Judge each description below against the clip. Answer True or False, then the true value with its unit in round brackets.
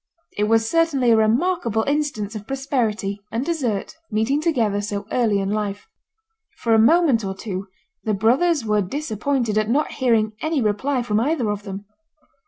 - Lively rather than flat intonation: False (4.8 semitones)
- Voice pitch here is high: True (225 Hz)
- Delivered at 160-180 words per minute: True (165 wpm)